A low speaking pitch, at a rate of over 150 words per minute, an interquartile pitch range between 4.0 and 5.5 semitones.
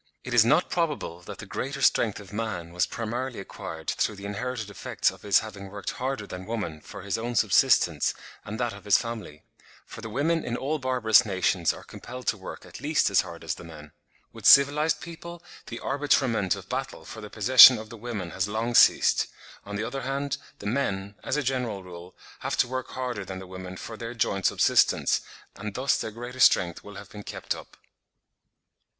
Yes: low, 110 Hz; fast, 205 wpm; average, 4.5 semitones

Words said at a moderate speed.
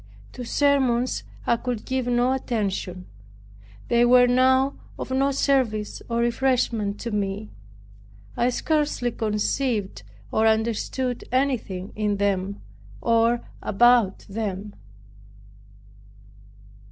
No: slow, 100 wpm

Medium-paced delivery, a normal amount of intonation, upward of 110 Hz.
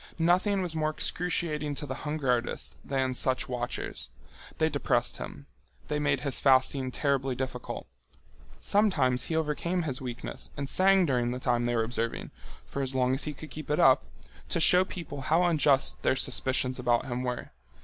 Yes: average, 175 wpm; average, 3.6 semitones; low, 135 Hz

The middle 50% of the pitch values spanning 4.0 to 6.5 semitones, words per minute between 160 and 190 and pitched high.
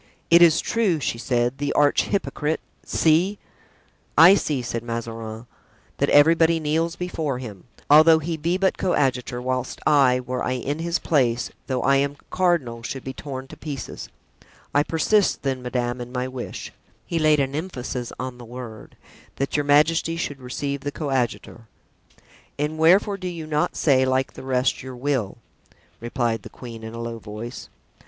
No: average, 4.4 semitones; average, 165 wpm; low, 135 Hz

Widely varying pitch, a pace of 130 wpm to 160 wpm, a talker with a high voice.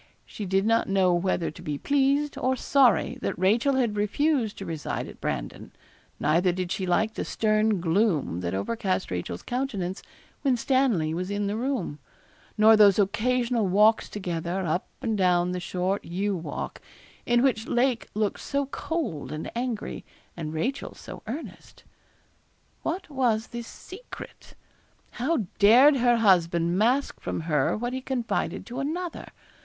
Yes: wide, 5.8 semitones; average, 150 wpm; high, 215 Hz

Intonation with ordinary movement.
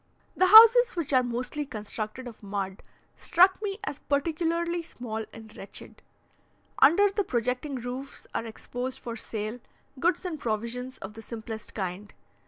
No: wide, 7.1 semitones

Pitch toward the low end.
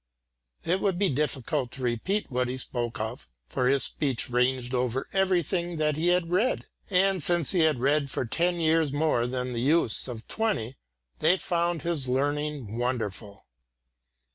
No: medium, 145 Hz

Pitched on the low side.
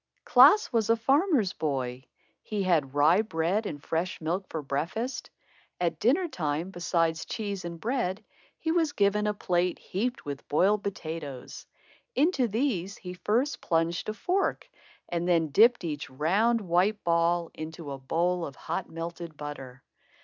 No: medium, 180 Hz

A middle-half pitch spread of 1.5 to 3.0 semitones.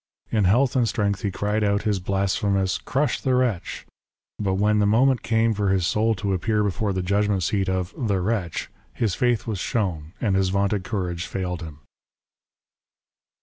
Yes: average, 2.7 semitones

